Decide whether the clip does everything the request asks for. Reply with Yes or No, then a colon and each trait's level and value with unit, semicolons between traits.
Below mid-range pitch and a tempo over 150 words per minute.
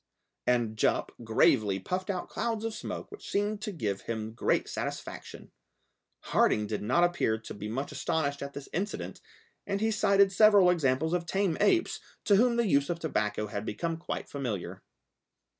No: medium, 160 Hz; average, 170 wpm